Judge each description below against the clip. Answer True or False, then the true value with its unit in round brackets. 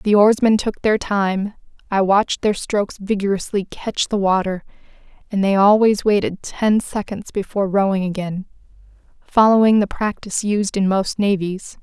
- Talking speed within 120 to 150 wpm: True (145 wpm)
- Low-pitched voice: False (200 Hz)